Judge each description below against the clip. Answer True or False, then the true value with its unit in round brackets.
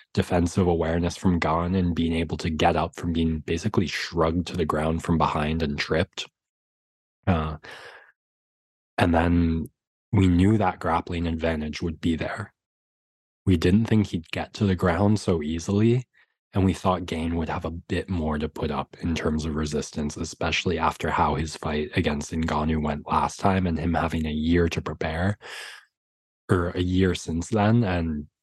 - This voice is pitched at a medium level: False (85 Hz)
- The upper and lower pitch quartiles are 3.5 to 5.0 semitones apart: False (2.7 semitones)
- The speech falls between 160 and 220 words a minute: True (170 wpm)